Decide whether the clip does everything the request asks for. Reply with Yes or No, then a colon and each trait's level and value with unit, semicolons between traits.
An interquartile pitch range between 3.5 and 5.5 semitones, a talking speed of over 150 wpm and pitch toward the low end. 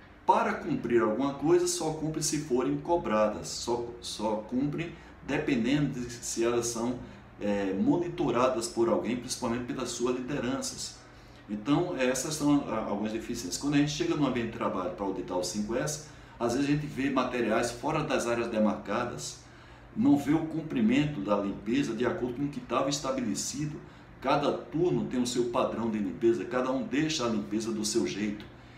Yes: average, 5.0 semitones; average, 170 wpm; low, 120 Hz